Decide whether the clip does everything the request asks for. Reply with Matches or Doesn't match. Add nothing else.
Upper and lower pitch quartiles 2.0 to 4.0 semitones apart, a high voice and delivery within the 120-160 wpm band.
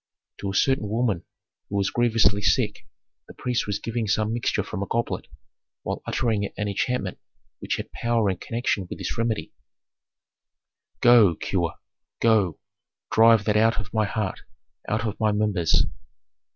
Doesn't match